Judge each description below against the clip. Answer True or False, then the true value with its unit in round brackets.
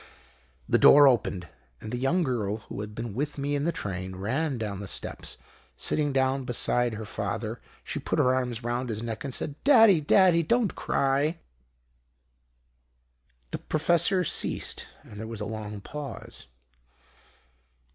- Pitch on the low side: True (130 Hz)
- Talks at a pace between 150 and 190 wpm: True (155 wpm)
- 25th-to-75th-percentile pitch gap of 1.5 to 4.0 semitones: False (5.5 semitones)